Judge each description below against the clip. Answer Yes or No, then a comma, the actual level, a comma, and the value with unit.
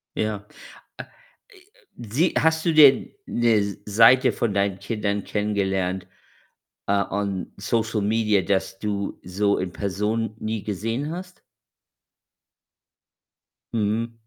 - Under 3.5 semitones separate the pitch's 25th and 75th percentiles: Yes, narrow, 2.5 semitones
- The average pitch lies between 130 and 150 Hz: No, low, 105 Hz